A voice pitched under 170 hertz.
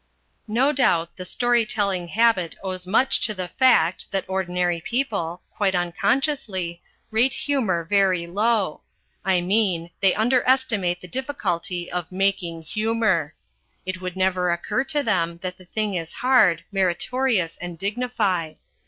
No: high, 190 Hz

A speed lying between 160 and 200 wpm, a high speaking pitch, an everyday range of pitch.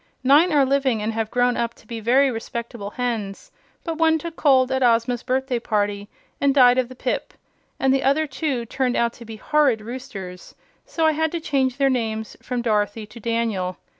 Yes: average, 195 wpm; high, 245 Hz; average, 3.4 semitones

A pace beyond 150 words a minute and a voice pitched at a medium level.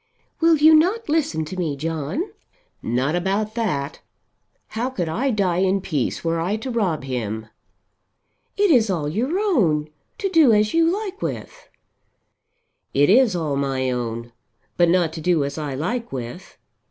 Yes: average, 160 wpm; medium, 180 Hz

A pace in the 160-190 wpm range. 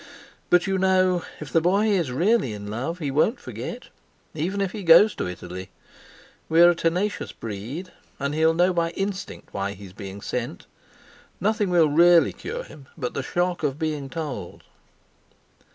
Yes: average, 165 wpm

